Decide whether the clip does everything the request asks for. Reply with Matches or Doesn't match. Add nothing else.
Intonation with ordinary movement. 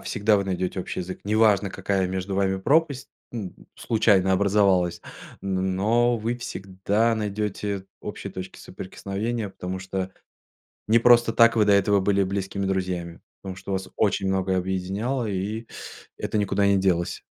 Doesn't match